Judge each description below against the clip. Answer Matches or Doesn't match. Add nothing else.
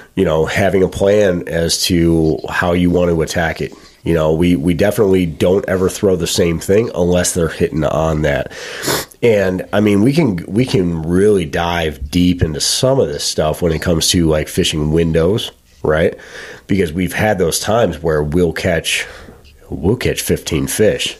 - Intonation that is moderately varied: Doesn't match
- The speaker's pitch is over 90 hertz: Doesn't match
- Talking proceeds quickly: Doesn't match